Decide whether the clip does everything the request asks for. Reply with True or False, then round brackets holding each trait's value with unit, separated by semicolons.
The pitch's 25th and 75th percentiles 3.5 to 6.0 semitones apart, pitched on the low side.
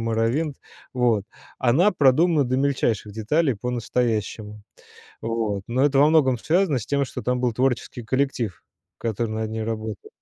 True (3.8 semitones; 125 Hz)